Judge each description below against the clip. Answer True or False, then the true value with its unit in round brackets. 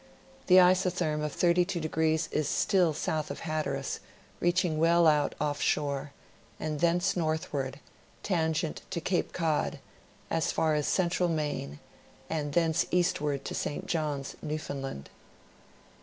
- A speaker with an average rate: False (125 wpm)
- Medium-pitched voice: True (160 Hz)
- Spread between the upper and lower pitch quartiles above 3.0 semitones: False (2.6 semitones)